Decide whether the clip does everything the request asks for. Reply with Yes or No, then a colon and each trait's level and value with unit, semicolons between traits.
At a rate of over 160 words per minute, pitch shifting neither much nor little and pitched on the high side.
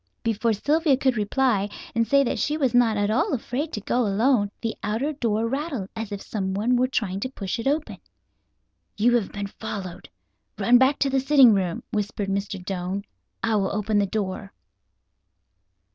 Yes: average, 175 wpm; average, 4.5 semitones; high, 225 Hz